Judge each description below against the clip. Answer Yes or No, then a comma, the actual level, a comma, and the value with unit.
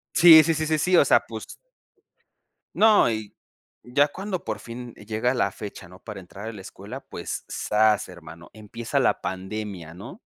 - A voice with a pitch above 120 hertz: No, low, 110 Hz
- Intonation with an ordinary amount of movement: No, wide, 6.5 semitones